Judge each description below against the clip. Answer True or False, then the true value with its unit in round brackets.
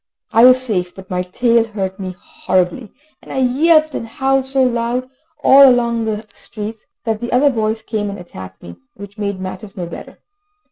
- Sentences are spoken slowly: False (185 wpm)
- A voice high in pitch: True (220 Hz)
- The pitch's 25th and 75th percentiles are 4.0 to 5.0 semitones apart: True (4.7 semitones)